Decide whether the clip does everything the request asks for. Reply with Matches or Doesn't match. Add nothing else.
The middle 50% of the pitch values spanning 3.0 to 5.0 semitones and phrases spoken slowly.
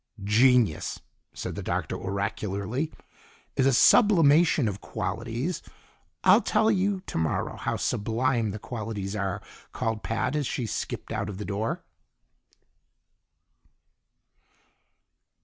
Doesn't match